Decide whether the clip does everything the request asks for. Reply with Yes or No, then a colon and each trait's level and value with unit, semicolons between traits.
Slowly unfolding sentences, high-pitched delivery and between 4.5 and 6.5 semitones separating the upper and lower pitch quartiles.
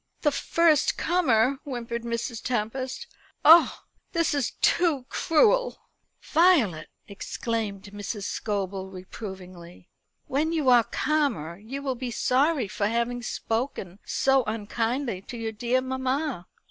Yes: slow, 120 wpm; high, 240 Hz; average, 5.2 semitones